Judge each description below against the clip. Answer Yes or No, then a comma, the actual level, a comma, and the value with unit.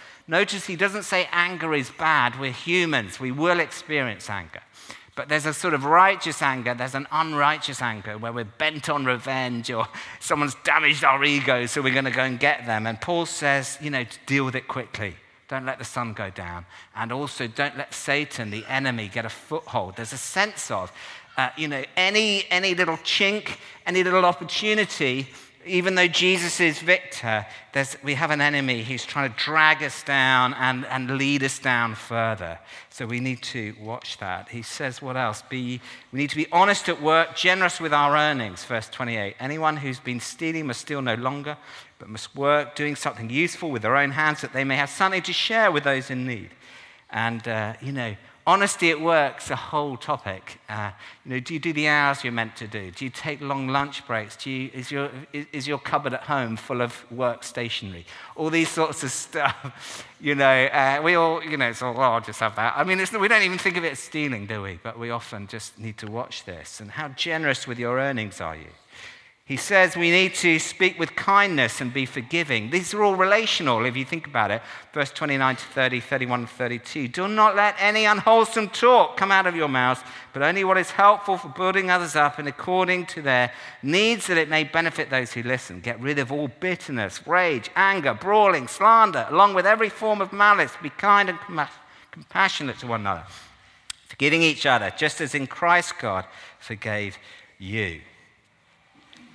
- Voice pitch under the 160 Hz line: Yes, medium, 140 Hz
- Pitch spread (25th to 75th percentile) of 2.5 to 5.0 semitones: No, wide, 5.5 semitones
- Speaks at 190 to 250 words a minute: Yes, fast, 205 wpm